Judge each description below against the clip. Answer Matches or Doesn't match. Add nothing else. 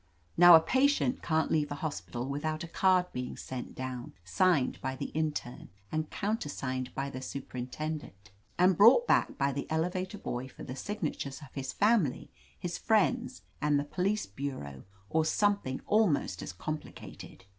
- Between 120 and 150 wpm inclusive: Doesn't match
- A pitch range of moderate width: Doesn't match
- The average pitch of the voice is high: Doesn't match